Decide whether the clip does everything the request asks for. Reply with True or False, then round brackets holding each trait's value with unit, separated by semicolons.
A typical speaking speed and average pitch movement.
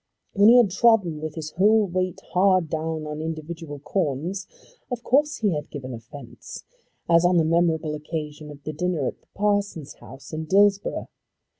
True (170 wpm; 4.5 semitones)